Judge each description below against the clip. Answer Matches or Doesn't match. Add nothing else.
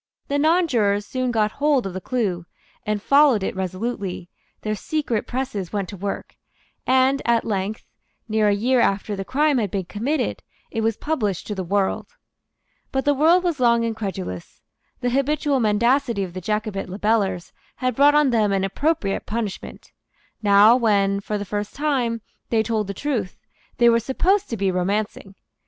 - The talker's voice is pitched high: Matches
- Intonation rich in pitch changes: Doesn't match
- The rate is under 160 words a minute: Doesn't match